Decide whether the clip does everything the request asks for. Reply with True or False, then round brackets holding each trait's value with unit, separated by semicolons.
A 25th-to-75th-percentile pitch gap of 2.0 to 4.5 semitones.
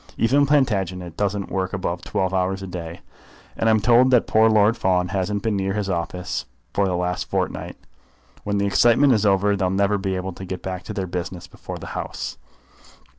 True (2.4 semitones)